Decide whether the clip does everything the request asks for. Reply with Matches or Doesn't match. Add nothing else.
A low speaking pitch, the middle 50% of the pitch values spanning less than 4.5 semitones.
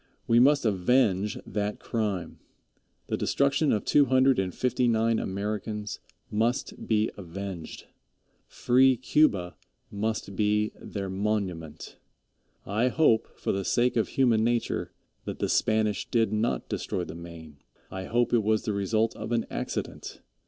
Matches